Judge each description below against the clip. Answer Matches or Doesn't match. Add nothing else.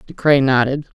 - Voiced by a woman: Matches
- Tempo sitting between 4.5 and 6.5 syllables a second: Matches